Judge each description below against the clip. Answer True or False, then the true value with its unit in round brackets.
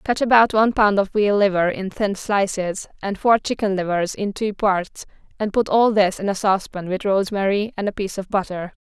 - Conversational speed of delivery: False (210 wpm)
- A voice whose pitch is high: True (200 Hz)